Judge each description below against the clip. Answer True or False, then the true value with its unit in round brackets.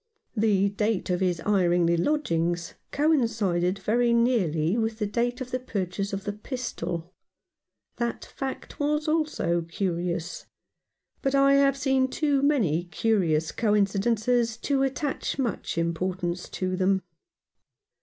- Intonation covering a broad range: True (6.3 semitones)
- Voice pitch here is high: True (210 Hz)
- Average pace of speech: False (125 wpm)